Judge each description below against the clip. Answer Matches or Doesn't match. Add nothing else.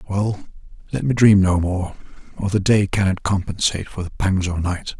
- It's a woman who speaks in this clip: Doesn't match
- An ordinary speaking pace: Matches